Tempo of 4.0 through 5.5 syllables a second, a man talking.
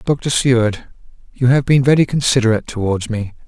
No: 5.7 syllables/s; male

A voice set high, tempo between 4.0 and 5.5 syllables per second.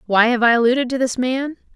No: very high, 250 Hz; 6.2 syllables/s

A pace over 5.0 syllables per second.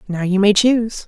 Yes: 5.5 syllables/s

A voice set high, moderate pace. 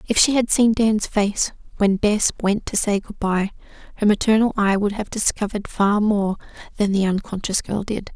Yes: high, 205 Hz; average, 190 wpm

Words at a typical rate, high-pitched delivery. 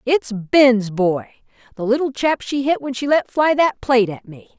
Yes: average, 195 wpm; high, 245 Hz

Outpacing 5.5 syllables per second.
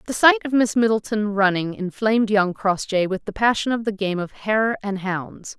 No: 4.8 syllables/s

